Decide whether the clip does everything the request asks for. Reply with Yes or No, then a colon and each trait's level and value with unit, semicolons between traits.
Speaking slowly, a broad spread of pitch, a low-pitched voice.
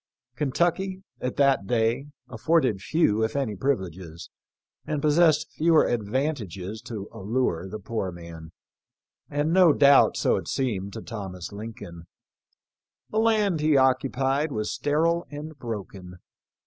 Yes: slow, 130 wpm; wide, 6.9 semitones; low, 125 Hz